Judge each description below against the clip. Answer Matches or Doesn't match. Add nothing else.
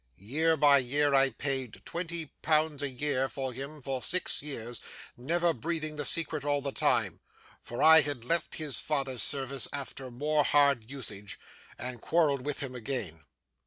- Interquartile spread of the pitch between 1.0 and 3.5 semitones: Matches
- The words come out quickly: Doesn't match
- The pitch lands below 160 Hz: Matches